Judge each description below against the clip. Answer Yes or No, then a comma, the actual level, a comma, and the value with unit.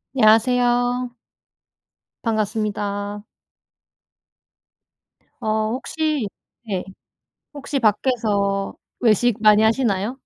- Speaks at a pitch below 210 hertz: No, high, 220 Hz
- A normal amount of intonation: Yes, average, 3.0 semitones